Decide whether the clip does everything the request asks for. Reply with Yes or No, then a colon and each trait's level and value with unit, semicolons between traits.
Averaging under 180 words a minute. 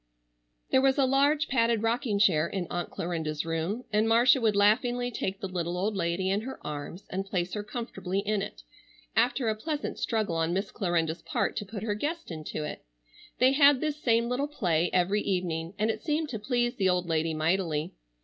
No: average, 195 wpm